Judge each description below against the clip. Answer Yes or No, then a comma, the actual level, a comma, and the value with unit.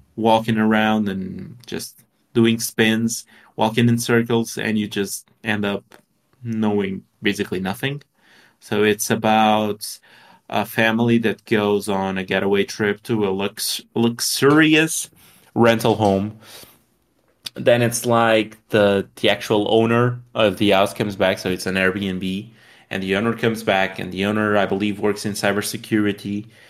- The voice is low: Yes, low, 105 Hz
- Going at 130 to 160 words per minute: Yes, average, 140 wpm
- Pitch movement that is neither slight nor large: No, narrow, 2.3 semitones